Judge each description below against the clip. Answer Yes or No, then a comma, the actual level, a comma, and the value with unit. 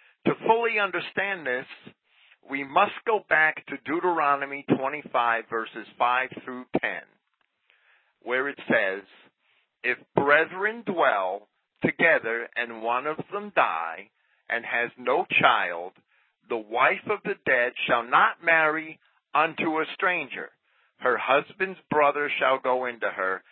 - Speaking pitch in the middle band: Yes, medium, 145 Hz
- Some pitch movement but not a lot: No, wide, 6.1 semitones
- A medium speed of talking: No, slow, 125 wpm